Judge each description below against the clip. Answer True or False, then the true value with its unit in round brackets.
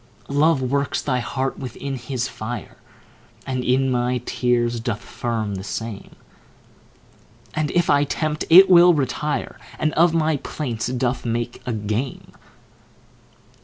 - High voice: False (130 Hz)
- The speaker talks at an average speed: False (130 wpm)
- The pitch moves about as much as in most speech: True (3.8 semitones)